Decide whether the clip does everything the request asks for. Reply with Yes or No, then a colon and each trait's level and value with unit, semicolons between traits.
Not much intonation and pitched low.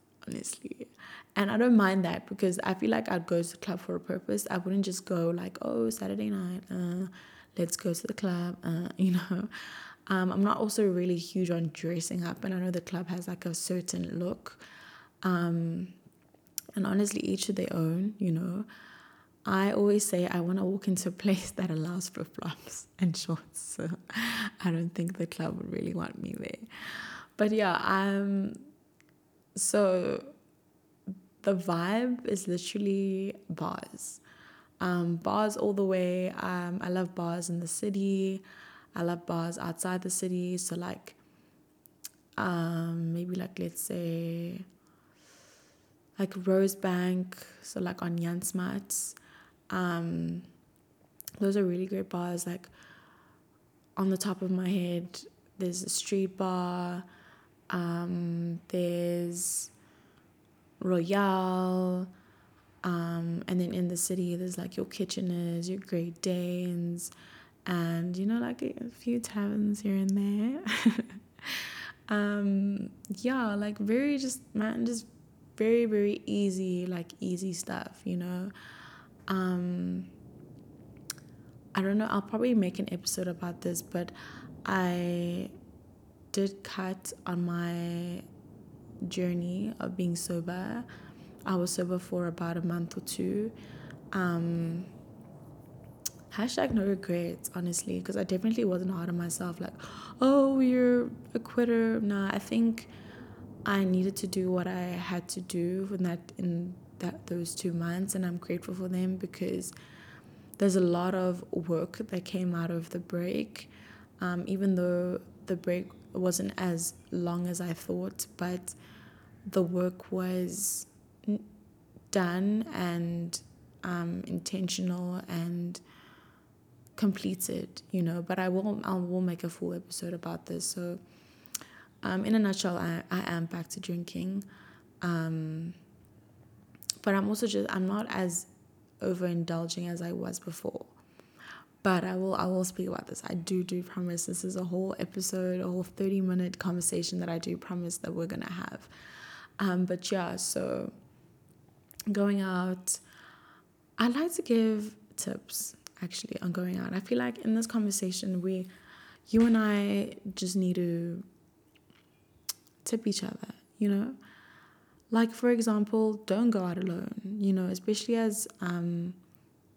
No: narrow, 2.3 semitones; medium, 180 Hz